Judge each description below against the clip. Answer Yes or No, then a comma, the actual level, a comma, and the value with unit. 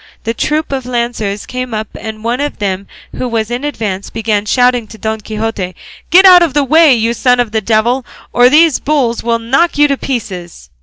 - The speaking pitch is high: Yes, high, 235 Hz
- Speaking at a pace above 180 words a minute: Yes, fast, 205 wpm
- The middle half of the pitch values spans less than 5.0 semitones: Yes, average, 3.6 semitones